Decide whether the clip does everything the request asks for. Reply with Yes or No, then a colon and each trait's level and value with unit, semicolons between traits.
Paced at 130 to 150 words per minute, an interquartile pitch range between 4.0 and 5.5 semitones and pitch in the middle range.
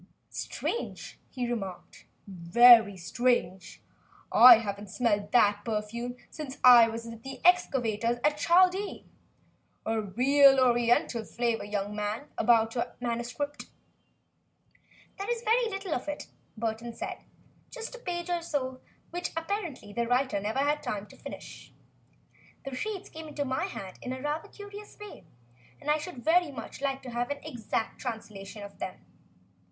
No: average, 145 wpm; average, 5.2 semitones; high, 245 Hz